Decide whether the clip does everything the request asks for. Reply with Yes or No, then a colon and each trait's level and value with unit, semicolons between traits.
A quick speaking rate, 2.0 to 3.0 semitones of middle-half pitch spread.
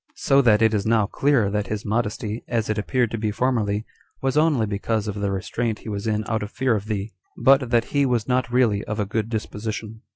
Yes: fast, 230 wpm; narrow, 2.4 semitones